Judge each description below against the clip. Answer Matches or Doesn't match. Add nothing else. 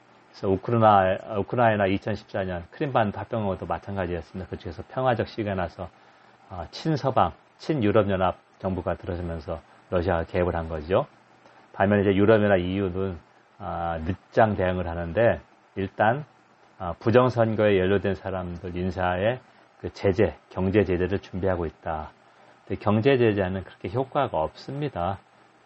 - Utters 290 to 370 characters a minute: Matches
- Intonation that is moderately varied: Matches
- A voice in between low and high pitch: Doesn't match